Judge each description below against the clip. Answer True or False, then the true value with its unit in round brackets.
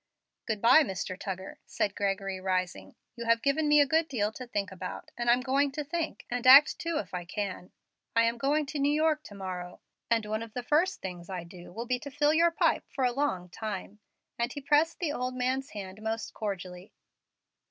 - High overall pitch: True (235 Hz)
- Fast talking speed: True (215 wpm)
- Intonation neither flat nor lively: False (6.6 semitones)